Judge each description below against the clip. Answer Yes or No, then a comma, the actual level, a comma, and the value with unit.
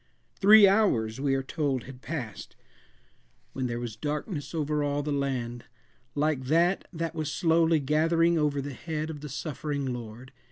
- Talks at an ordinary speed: Yes, average, 160 wpm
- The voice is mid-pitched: Yes, medium, 145 Hz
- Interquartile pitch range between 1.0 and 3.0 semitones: No, average, 3.6 semitones